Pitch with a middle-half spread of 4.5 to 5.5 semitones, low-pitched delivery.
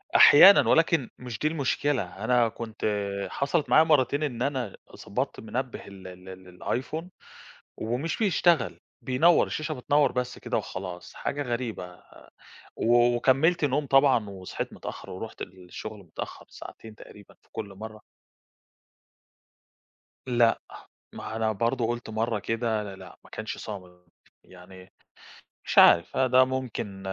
Yes: average, 4.9 semitones; low, 120 Hz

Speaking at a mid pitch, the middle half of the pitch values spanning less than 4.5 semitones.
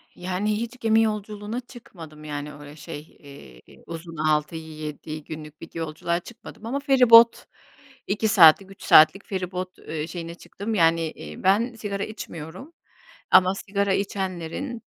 No: medium, 180 Hz; average, 5.2 semitones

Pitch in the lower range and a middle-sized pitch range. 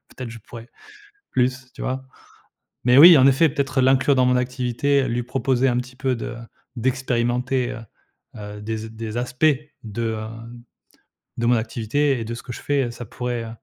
No: low, 125 Hz; narrow, 2.1 semitones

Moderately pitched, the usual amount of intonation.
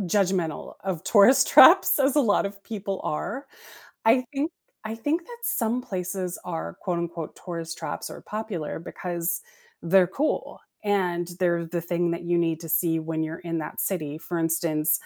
Yes: medium, 175 Hz; average, 3.8 semitones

